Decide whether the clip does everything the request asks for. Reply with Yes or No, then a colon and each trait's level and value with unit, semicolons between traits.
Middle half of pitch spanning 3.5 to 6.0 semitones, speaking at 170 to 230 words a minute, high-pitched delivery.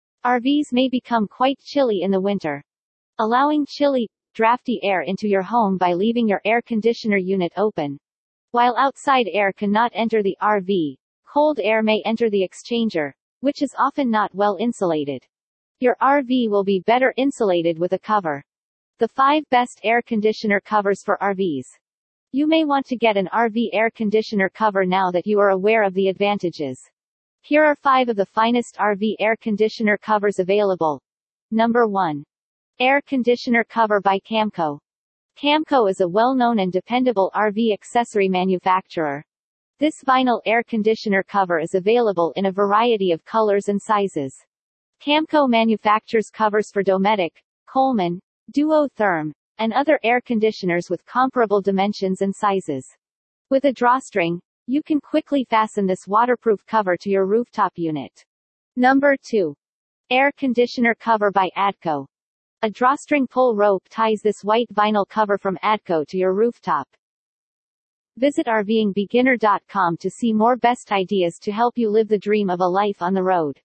No: average, 4.0 semitones; average, 150 wpm; high, 215 Hz